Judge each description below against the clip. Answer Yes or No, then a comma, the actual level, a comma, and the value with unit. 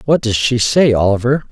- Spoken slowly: No, average, 200 wpm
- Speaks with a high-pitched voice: No, low, 125 Hz